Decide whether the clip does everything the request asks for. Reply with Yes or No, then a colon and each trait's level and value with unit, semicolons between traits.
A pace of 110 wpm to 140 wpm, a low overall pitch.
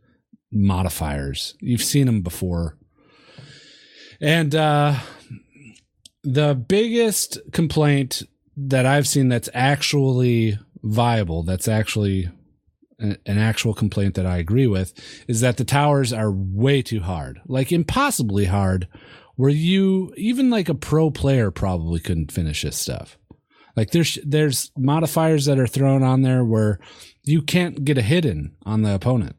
Yes: slow, 135 wpm; low, 125 Hz